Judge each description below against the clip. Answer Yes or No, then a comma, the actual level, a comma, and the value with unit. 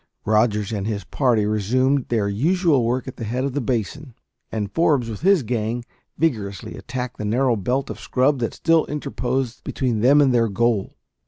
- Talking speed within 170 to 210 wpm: Yes, average, 180 wpm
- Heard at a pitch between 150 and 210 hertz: No, low, 120 Hz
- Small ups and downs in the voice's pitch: No, average, 4.0 semitones